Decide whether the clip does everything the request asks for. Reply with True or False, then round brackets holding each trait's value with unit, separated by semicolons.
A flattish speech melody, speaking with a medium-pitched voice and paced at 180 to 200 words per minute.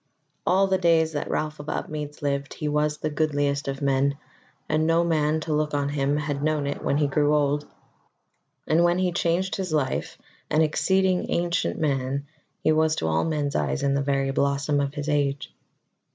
True (2.0 semitones; 150 Hz; 190 wpm)